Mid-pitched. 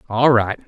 No: low, 115 Hz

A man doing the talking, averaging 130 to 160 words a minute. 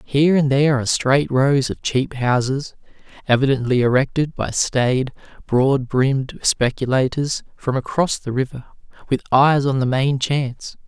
Yes: male; average, 145 wpm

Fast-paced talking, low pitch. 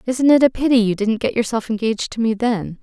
No: fast, 255 wpm; high, 230 Hz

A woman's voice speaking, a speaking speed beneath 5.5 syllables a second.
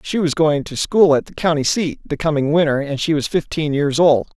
No: male; 5.3 syllables/s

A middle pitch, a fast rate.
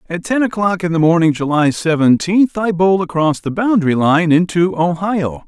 No: medium, 175 Hz; average, 175 wpm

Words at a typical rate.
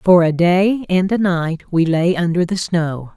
No: fast, 210 wpm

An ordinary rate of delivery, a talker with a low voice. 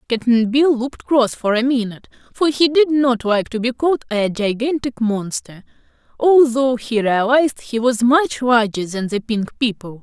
No: average, 175 wpm; high, 240 Hz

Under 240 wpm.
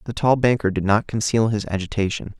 Yes: average, 200 wpm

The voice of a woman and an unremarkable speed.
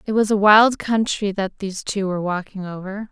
No: female; fast, 210 wpm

